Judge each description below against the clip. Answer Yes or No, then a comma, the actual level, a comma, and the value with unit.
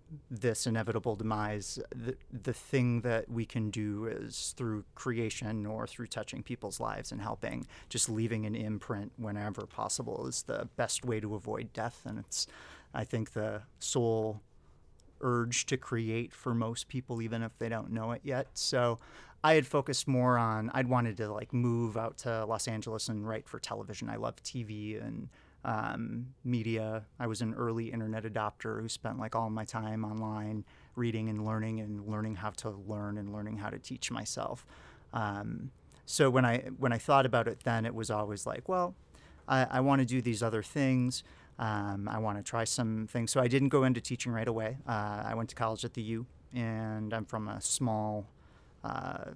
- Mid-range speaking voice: No, low, 115 Hz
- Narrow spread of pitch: Yes, narrow, 2.2 semitones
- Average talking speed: Yes, average, 190 wpm